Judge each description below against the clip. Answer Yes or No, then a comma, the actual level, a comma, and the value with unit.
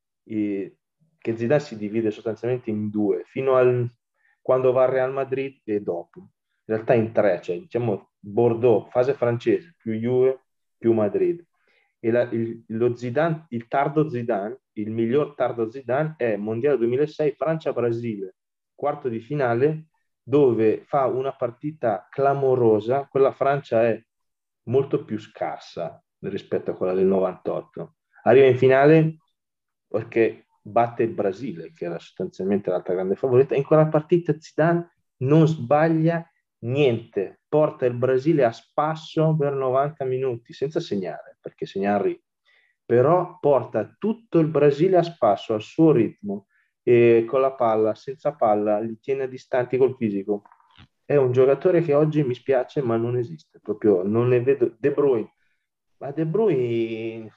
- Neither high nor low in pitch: No, low, 130 Hz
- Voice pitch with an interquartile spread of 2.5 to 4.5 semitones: No, average, 5.0 semitones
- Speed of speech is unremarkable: Yes, average, 140 wpm